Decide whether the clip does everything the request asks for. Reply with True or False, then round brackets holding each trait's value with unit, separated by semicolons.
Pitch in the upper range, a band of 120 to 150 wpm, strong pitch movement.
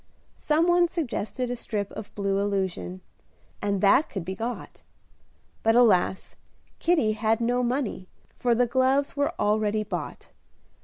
False (225 Hz; 140 wpm; 4.3 semitones)